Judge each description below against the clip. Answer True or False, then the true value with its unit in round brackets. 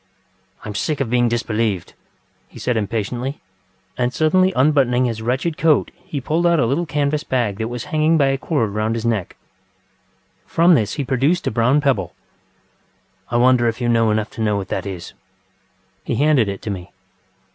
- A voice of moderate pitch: False (125 Hz)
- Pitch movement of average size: True (4.8 semitones)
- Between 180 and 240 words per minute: True (190 wpm)